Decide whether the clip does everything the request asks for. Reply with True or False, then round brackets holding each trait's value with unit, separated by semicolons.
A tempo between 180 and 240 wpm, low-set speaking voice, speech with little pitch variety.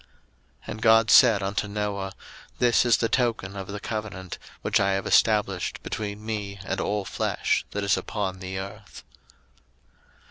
False (155 wpm; 105 Hz; 2.1 semitones)